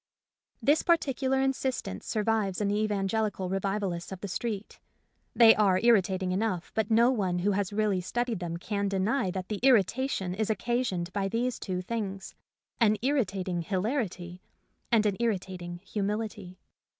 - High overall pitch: Yes, high, 205 Hz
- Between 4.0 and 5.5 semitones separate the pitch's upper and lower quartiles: No, average, 3.5 semitones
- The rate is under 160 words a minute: Yes, average, 150 wpm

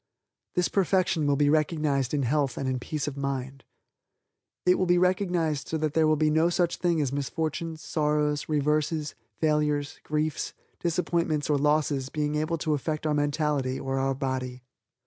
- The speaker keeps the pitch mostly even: Yes, narrow, 2.1 semitones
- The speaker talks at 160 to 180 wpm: Yes, average, 165 wpm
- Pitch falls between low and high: Yes, medium, 150 Hz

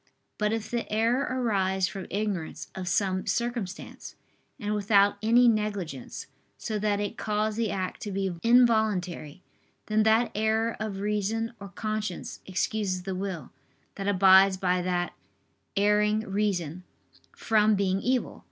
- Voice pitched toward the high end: Yes, high, 205 Hz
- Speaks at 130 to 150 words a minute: Yes, slow, 135 wpm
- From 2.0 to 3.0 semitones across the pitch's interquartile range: Yes, narrow, 2.4 semitones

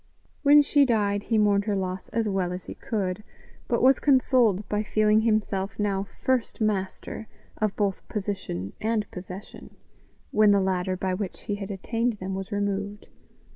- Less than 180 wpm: Yes, average, 165 wpm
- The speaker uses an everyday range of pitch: No, narrow, 2.3 semitones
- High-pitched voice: Yes, high, 205 Hz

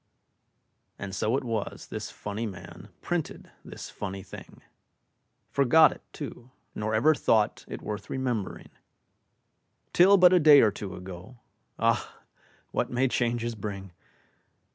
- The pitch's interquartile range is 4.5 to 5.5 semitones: Yes, average, 5.2 semitones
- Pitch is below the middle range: Yes, low, 115 Hz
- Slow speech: Yes, slow, 130 wpm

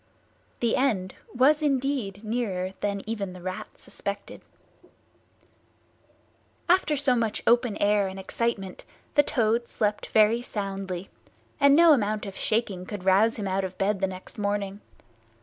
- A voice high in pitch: Yes, high, 210 Hz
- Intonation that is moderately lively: Yes, average, 3.7 semitones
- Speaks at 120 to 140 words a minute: Yes, slow, 135 wpm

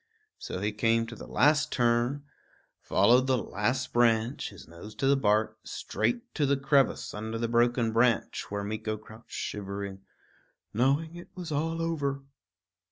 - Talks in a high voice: No, low, 120 Hz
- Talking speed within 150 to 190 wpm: Yes, average, 155 wpm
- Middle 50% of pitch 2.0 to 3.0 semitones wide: No, average, 4.5 semitones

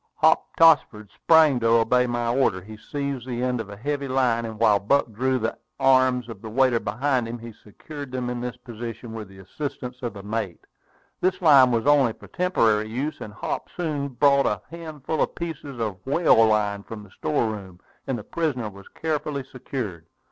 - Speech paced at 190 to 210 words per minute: Yes, average, 195 wpm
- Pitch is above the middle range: No, low, 125 Hz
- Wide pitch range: No, average, 4.2 semitones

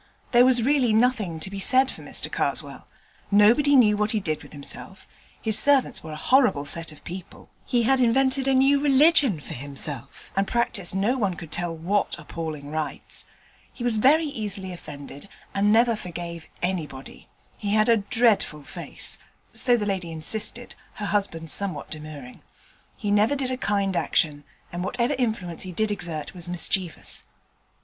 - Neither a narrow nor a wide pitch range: No, wide, 6.5 semitones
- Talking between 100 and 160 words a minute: No, average, 170 wpm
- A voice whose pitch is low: No, high, 200 Hz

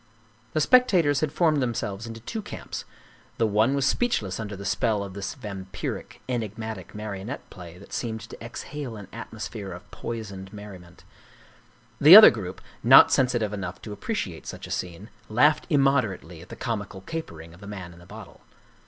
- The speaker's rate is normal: Yes, average, 180 wpm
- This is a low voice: Yes, low, 110 Hz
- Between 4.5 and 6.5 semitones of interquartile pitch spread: Yes, average, 5.2 semitones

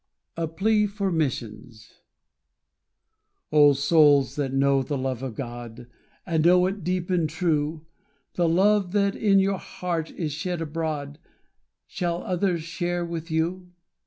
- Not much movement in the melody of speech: No, average, 3.9 semitones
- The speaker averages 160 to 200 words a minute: No, slow, 135 wpm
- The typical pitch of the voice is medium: Yes, medium, 165 Hz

